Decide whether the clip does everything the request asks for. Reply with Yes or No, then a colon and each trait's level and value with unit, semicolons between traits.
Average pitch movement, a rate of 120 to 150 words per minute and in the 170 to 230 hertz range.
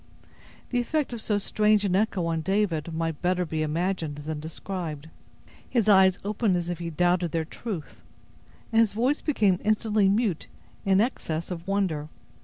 No: average, 4.5 semitones; average, 165 wpm; medium, 185 Hz